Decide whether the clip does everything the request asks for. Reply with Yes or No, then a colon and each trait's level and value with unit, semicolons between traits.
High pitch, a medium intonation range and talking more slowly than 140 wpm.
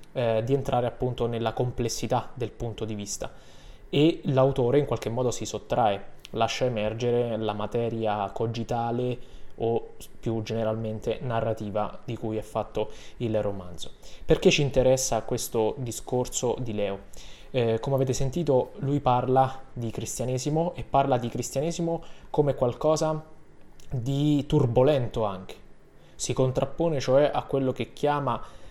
No: low, 125 Hz; average, 3.3 semitones; average, 130 wpm